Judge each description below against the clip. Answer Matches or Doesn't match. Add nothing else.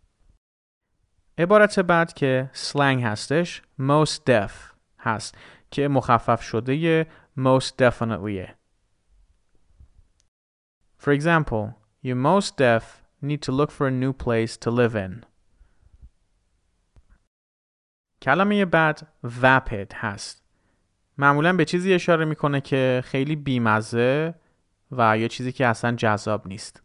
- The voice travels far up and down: Matches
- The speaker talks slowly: Matches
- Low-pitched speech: Matches